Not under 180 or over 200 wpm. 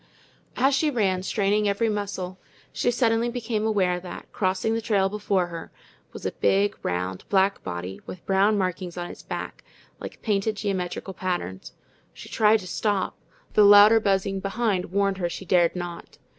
No: average, 170 wpm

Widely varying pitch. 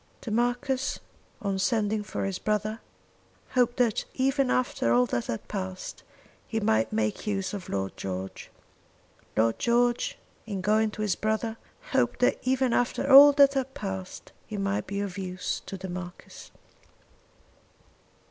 No: average, 4.5 semitones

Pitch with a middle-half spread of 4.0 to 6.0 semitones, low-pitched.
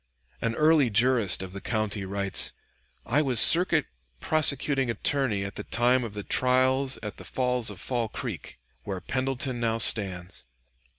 Yes: average, 4.4 semitones; low, 120 Hz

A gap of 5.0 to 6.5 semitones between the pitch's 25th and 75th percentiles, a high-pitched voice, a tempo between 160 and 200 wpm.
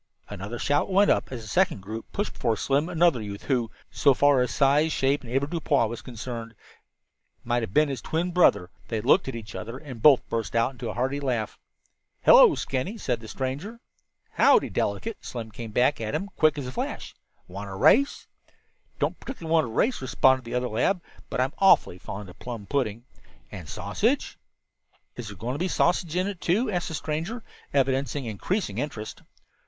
No: wide, 5.5 semitones; low, 130 Hz; average, 190 wpm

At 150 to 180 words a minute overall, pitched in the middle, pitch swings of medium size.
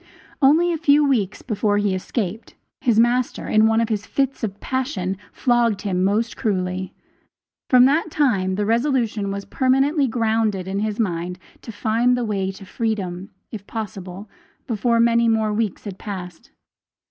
No: average, 160 wpm; high, 220 Hz; average, 3.7 semitones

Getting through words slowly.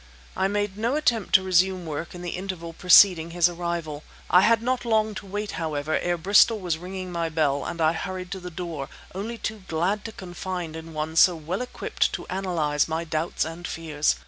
No: average, 200 wpm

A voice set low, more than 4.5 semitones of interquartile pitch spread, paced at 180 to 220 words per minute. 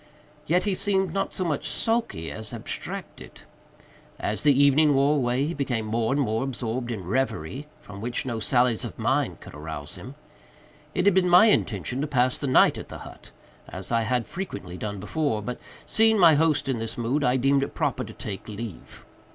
Yes: low, 130 Hz; average, 5.2 semitones; average, 195 wpm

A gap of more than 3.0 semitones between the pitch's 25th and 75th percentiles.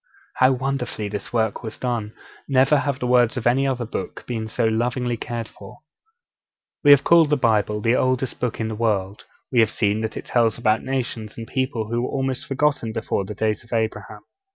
No: average, 2.7 semitones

